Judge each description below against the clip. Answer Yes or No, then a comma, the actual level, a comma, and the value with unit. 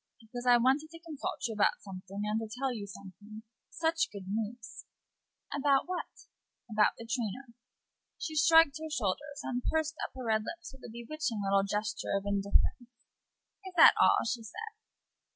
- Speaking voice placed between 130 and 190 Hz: No, high, 240 Hz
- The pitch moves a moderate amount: No, wide, 6.1 semitones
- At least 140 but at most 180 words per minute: Yes, average, 170 wpm